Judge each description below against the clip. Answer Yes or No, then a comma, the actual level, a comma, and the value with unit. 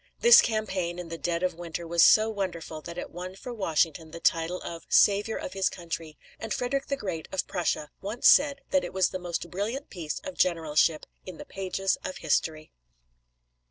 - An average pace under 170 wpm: No, average, 195 wpm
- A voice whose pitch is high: No, medium, 180 Hz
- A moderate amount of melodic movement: Yes, average, 3.9 semitones